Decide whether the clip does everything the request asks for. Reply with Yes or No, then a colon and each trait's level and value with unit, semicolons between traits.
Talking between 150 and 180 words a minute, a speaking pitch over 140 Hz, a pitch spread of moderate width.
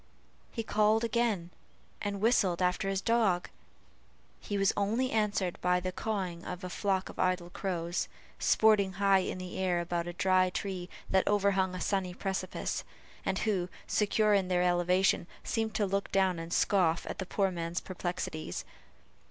No: average, 160 wpm; high, 190 Hz; narrow, 2.2 semitones